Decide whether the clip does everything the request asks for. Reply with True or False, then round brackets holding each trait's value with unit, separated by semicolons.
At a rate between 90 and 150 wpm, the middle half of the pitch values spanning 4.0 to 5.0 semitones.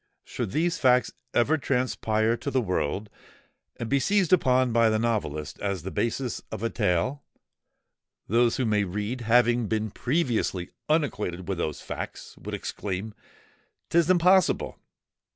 True (140 wpm; 4.4 semitones)